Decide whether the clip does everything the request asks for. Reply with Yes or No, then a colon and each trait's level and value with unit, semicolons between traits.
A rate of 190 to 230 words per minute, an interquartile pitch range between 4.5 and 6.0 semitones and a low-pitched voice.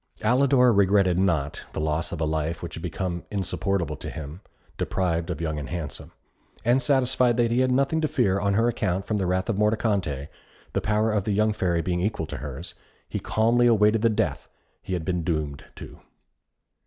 Yes: average, 195 wpm; average, 5.0 semitones; very low, 95 Hz